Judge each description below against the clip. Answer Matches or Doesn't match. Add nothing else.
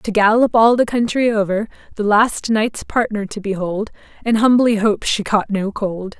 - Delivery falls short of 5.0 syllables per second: Matches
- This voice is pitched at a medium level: Doesn't match